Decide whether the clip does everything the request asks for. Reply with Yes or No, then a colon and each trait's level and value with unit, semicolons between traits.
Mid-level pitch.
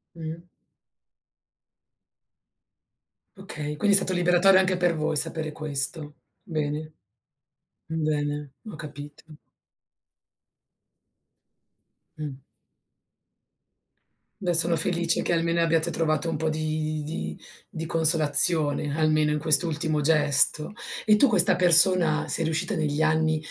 Yes: medium, 160 Hz